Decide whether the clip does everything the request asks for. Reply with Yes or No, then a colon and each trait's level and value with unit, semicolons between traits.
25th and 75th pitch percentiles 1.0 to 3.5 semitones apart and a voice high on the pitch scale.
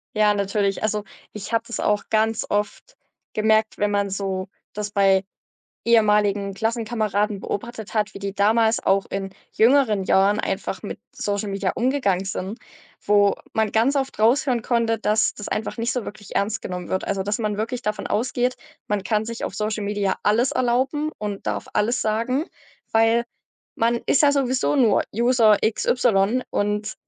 Yes: narrow, 2.4 semitones; high, 215 Hz